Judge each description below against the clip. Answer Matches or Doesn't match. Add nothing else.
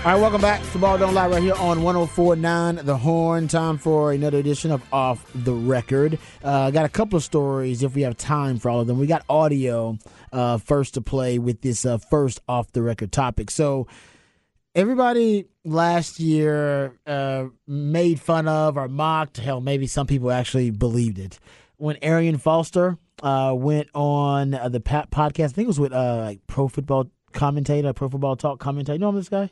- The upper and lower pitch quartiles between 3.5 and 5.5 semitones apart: Matches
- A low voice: Doesn't match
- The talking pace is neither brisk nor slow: Matches